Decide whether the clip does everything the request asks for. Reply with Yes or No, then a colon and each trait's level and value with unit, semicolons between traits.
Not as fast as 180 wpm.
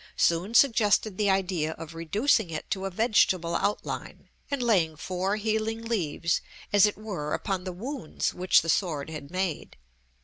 Yes: average, 160 wpm